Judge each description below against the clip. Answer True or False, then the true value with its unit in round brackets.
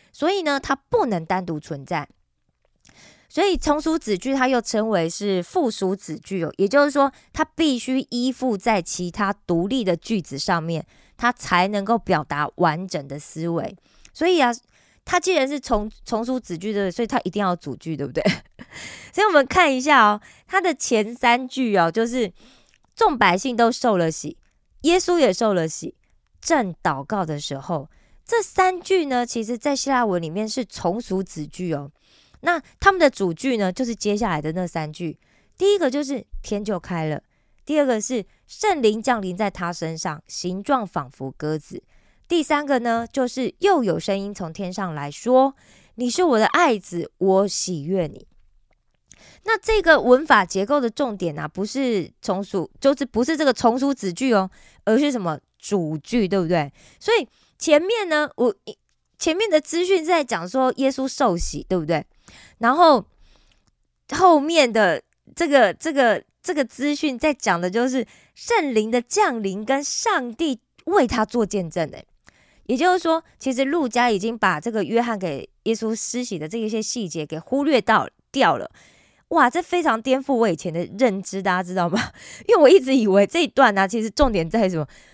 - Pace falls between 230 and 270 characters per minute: True (250 characters per minute)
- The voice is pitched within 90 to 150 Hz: False (230 Hz)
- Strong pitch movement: True (7.2 semitones)